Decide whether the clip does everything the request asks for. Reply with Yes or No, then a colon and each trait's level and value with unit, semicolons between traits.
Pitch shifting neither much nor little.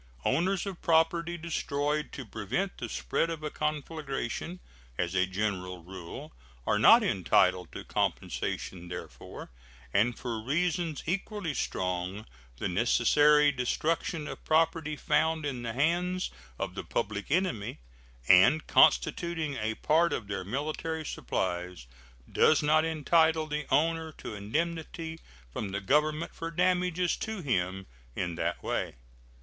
No: wide, 7.4 semitones